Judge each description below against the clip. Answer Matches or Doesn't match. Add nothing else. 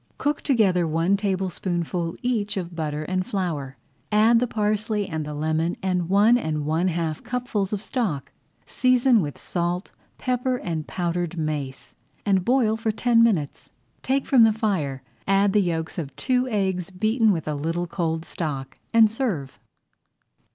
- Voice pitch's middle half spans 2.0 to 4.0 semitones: Doesn't match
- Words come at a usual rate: Matches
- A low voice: Doesn't match